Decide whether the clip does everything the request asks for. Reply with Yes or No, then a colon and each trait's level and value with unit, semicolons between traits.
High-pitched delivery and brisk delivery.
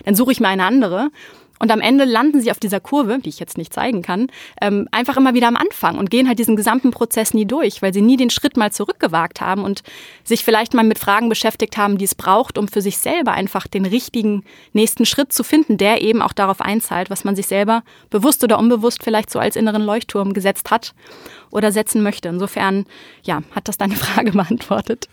Yes: high, 220 Hz; fast, 220 wpm